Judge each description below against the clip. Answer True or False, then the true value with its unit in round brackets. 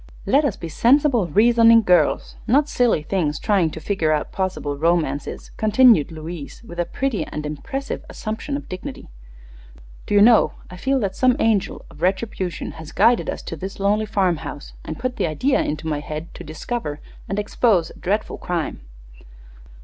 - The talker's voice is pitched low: False (190 Hz)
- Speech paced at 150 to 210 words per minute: True (170 wpm)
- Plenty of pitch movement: True (6.4 semitones)